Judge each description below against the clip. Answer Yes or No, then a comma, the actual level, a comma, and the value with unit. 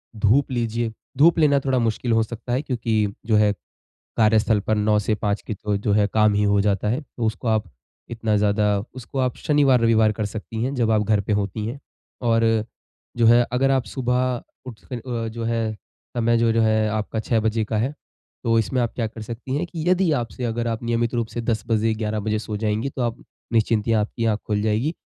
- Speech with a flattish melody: Yes, narrow, 2.0 semitones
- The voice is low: Yes, low, 115 Hz